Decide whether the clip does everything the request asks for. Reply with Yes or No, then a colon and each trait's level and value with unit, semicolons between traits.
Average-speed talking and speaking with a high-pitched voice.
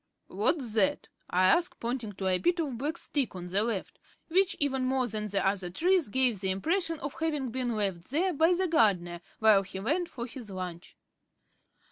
Yes: average, 190 wpm; high, 235 Hz